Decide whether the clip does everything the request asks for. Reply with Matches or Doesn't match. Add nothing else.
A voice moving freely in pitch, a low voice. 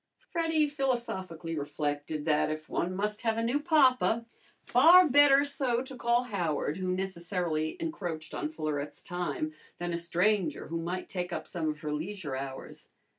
Doesn't match